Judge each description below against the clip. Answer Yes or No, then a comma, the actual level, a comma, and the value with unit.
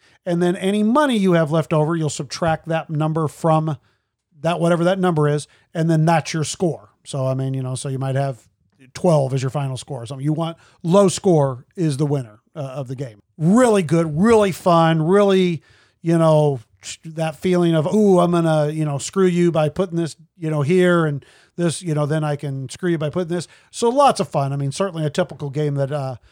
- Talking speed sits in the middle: No, fast, 225 wpm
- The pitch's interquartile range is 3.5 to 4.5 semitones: Yes, average, 3.8 semitones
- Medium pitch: Yes, medium, 155 Hz